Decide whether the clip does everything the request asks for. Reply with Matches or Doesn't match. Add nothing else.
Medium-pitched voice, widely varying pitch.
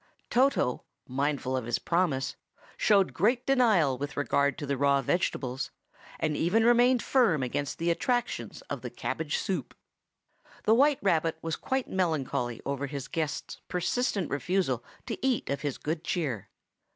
Matches